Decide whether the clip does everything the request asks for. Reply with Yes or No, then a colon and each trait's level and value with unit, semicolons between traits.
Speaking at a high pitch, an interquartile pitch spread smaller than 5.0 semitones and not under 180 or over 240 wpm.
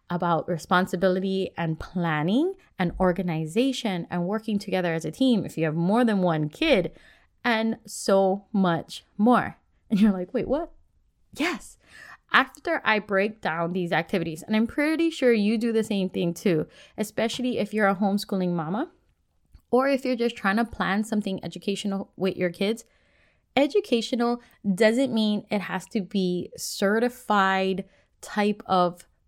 No: high, 200 Hz; average, 4.4 semitones; average, 150 wpm